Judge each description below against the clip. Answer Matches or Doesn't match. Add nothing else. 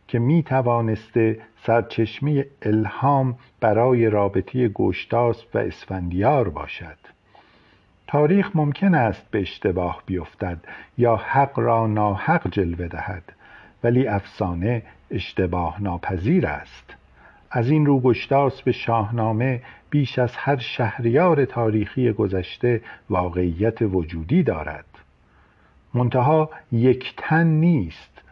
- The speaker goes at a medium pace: Doesn't match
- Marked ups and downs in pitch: Doesn't match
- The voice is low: Matches